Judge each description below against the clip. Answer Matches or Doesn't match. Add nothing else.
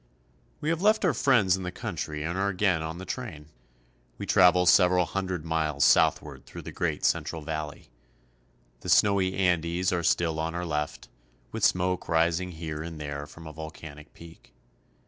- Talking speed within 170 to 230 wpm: Matches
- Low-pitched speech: Matches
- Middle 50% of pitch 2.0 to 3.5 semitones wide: Matches